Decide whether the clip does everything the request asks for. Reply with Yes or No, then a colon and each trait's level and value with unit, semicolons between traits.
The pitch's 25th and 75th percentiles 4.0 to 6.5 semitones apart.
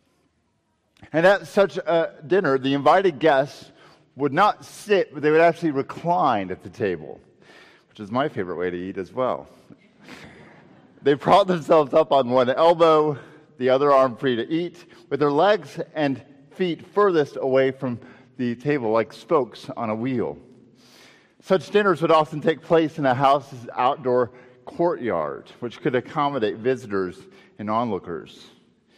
Yes: average, 4.3 semitones